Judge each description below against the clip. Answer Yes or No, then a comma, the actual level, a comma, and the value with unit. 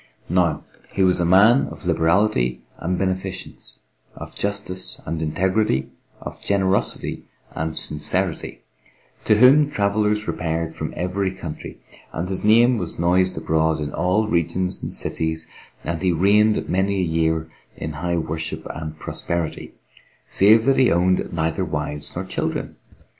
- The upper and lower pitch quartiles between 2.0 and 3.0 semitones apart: No, average, 3.6 semitones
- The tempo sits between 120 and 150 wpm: Yes, average, 140 wpm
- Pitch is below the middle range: Yes, very low, 90 Hz